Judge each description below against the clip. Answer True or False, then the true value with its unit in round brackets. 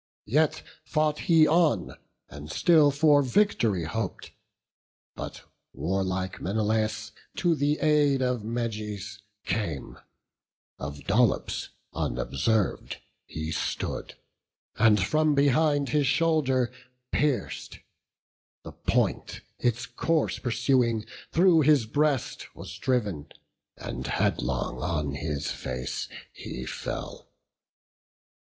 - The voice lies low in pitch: True (120 Hz)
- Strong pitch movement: True (7.3 semitones)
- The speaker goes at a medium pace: False (95 wpm)